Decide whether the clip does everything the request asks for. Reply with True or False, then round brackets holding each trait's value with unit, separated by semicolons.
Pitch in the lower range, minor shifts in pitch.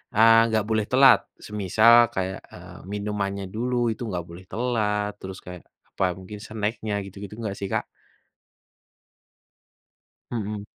True (105 Hz; 2.1 semitones)